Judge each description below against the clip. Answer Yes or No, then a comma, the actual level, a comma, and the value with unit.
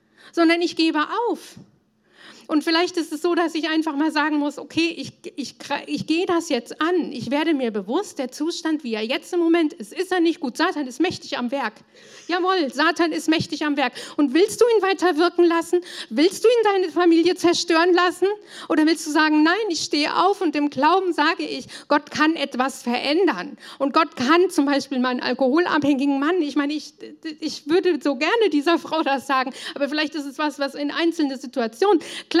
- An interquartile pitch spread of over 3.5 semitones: No, average, 3.2 semitones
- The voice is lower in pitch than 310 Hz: No, very high, 315 Hz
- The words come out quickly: Yes, fast, 200 wpm